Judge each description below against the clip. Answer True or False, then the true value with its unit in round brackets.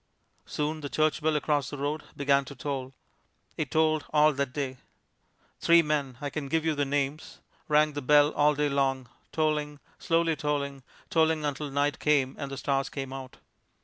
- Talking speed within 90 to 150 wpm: False (180 wpm)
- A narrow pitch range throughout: True (1.7 semitones)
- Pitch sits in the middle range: True (145 Hz)